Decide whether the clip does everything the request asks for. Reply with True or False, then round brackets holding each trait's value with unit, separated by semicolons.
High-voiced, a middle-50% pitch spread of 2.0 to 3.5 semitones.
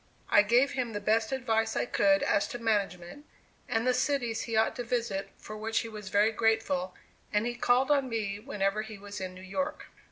True (220 Hz; 3.1 semitones)